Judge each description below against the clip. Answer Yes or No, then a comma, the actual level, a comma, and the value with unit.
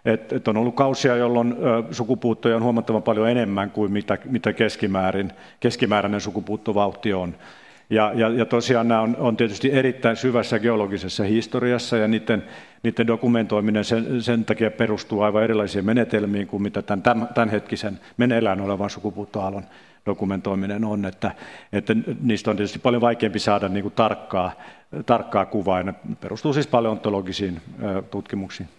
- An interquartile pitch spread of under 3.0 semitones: Yes, narrow, 2.4 semitones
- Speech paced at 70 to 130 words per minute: No, average, 145 wpm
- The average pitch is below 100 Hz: No, low, 110 Hz